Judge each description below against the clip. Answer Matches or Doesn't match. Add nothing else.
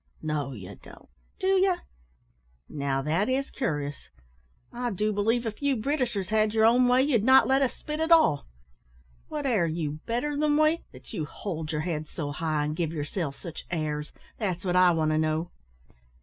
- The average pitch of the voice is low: Doesn't match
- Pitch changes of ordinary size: Doesn't match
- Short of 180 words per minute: Doesn't match